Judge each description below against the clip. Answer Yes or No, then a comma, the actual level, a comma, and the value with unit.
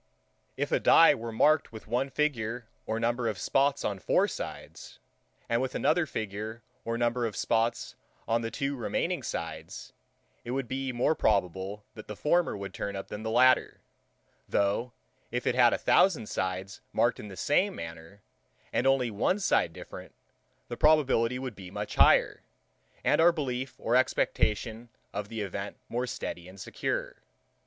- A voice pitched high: No, low, 115 Hz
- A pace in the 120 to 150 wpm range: No, average, 165 wpm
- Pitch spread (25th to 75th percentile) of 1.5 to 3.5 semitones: No, average, 3.9 semitones